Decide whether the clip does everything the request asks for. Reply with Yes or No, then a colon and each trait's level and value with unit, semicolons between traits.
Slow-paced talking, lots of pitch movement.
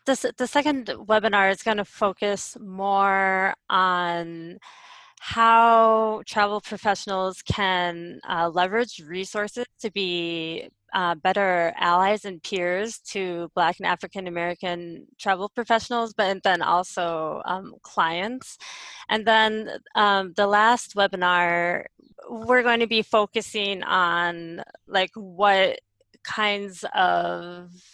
No: slow, 115 wpm; average, 3.8 semitones